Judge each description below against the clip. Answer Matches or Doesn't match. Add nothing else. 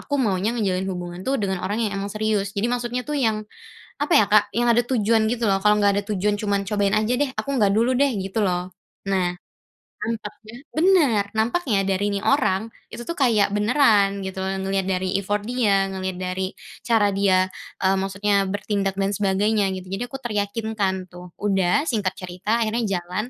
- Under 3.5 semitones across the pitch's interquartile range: Matches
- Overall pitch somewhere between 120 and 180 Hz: Doesn't match